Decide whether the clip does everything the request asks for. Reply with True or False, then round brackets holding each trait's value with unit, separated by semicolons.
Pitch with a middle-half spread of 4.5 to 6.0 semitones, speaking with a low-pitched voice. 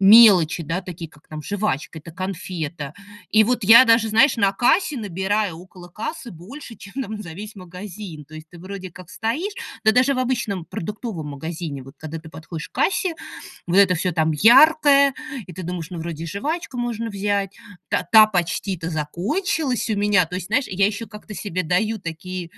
False (5.0 semitones; 195 Hz)